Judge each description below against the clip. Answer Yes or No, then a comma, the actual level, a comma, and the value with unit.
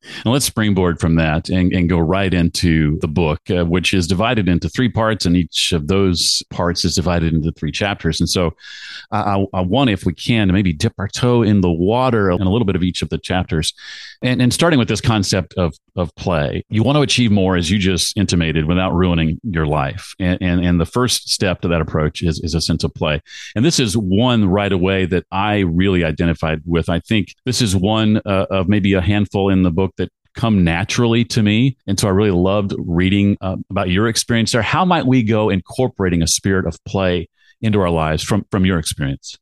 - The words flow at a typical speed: No, fast, 225 wpm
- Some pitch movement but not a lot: Yes, average, 3.8 semitones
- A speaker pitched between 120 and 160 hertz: No, very low, 95 Hz